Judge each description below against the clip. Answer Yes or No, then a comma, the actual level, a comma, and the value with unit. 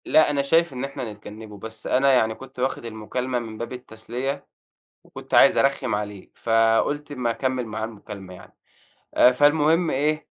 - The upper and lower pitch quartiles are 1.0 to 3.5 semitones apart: No, average, 3.9 semitones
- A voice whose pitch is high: No, low, 125 Hz